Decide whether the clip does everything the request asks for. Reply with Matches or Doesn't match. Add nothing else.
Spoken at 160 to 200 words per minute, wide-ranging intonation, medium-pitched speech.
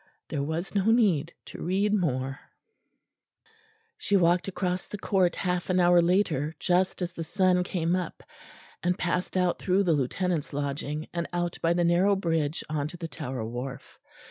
Doesn't match